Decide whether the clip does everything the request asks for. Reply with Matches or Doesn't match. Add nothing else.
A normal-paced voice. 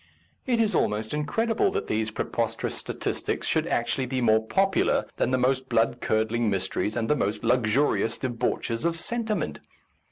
Matches